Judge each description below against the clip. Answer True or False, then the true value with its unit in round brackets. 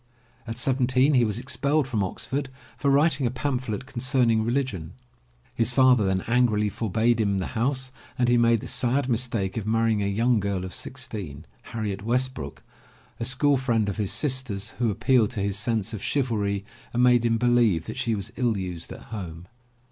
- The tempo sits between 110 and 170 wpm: False (185 wpm)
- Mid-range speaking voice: False (115 Hz)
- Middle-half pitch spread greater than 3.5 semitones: True (4.0 semitones)